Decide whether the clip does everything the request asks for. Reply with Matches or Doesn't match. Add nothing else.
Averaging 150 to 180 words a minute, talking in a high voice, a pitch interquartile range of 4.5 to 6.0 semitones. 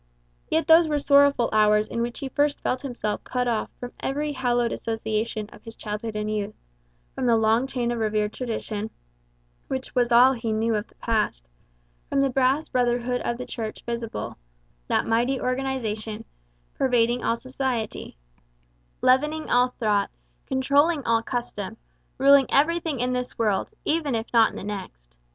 Doesn't match